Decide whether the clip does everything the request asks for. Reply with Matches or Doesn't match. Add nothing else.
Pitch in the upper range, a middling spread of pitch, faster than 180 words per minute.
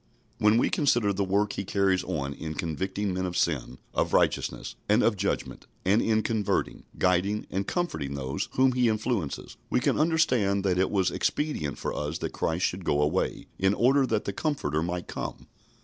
Doesn't match